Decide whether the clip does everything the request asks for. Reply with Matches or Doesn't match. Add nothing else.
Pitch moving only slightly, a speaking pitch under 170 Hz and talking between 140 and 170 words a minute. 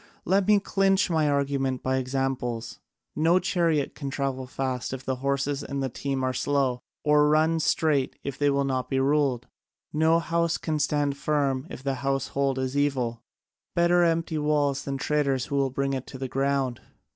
Doesn't match